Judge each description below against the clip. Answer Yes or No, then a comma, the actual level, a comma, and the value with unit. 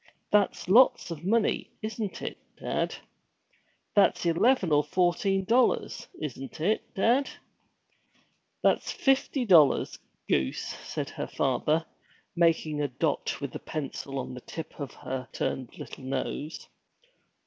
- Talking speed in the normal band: No, slow, 125 wpm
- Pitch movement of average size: No, wide, 6.6 semitones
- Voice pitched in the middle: Yes, medium, 165 Hz